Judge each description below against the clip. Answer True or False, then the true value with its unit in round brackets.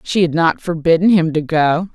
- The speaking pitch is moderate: True (165 Hz)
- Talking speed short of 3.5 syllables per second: False (4.9 syllables/s)